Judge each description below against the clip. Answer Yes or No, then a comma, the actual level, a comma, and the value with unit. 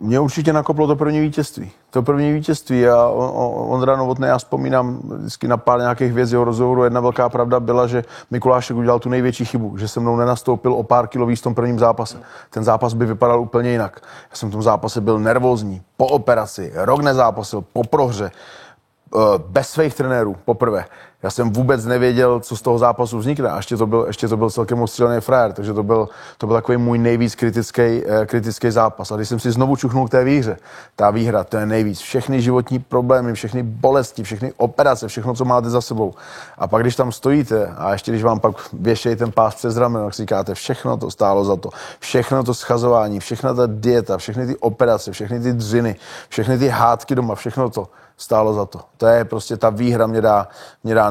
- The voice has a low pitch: Yes, low, 120 Hz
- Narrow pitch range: Yes, narrow, 1.9 semitones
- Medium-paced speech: No, fast, 205 wpm